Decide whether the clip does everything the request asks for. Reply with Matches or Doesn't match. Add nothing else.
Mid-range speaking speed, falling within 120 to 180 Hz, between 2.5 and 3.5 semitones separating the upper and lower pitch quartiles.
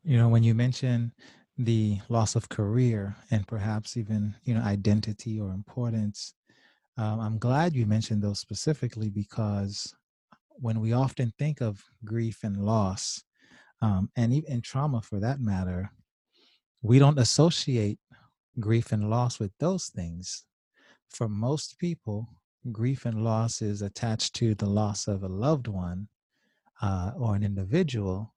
Doesn't match